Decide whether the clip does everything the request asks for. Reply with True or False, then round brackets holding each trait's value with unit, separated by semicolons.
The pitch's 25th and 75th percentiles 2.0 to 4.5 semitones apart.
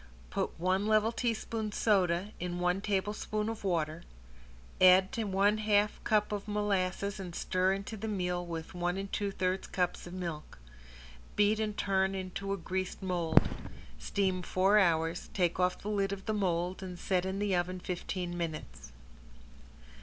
True (2.5 semitones)